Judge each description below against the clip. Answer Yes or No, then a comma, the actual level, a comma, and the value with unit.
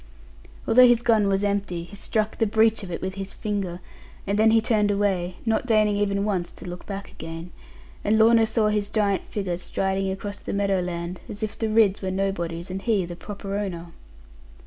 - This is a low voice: No, high, 200 Hz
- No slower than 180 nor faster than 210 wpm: Yes, average, 200 wpm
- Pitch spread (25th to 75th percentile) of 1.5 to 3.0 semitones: Yes, narrow, 2.4 semitones